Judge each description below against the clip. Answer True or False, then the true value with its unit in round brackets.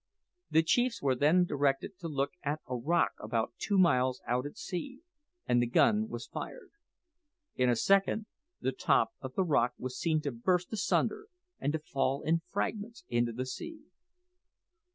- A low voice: False (150 Hz)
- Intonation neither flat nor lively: False (7.3 semitones)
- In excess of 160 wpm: True (170 wpm)